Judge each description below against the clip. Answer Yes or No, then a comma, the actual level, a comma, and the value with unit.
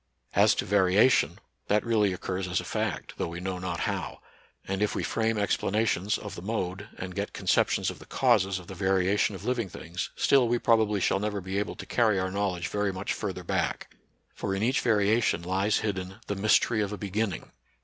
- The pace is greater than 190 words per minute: Yes, fast, 205 wpm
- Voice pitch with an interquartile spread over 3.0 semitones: No, narrow, 2.4 semitones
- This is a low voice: Yes, low, 100 Hz